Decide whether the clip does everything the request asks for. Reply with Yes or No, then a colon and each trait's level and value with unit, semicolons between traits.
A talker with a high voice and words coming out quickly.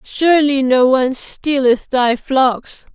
No: very high, 265 Hz; slow, 120 wpm